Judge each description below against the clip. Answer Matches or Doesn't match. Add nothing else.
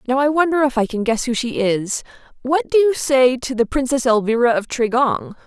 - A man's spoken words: Doesn't match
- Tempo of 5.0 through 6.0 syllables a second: Matches